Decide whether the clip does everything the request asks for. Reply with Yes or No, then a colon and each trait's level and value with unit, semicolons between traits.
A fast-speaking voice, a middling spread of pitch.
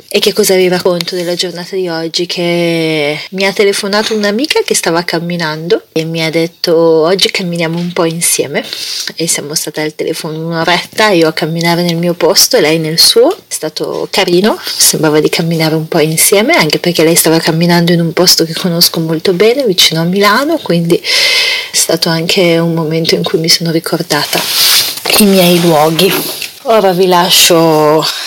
Yes: fast, 175 wpm; average, 3.2 semitones